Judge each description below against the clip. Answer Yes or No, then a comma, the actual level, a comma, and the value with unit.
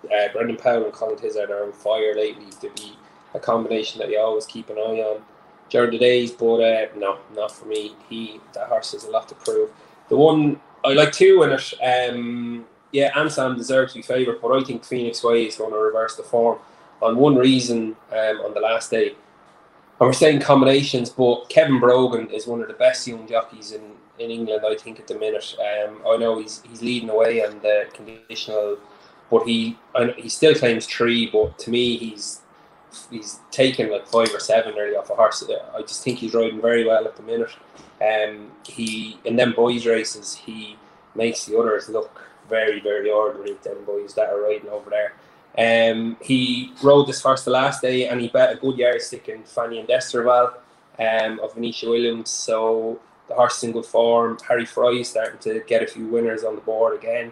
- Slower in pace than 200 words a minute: No, fast, 205 wpm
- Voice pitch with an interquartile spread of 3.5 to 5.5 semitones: No, average, 2.7 semitones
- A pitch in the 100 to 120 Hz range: Yes, low, 115 Hz